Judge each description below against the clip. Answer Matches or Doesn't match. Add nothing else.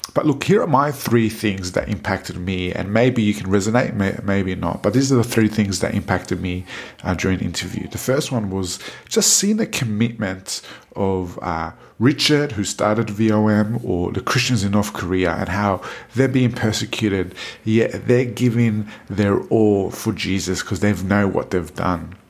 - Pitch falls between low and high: Doesn't match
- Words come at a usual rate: Matches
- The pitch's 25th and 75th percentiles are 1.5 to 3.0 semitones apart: Doesn't match